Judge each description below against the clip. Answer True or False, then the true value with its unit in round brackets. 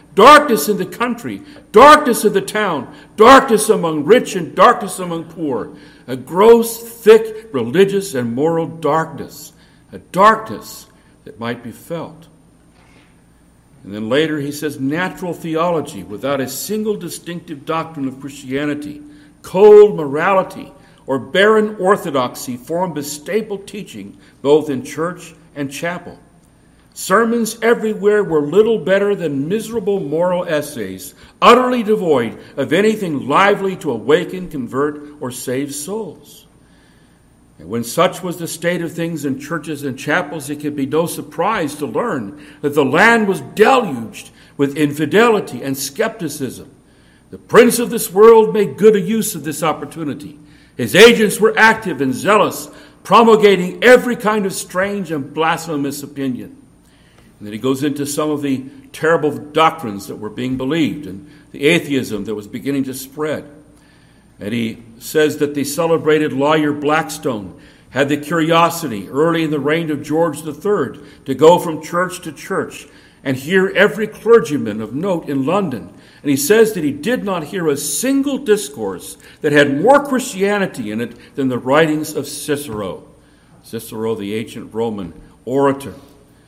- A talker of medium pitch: True (160 Hz)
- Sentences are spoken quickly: False (145 wpm)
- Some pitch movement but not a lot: False (6.1 semitones)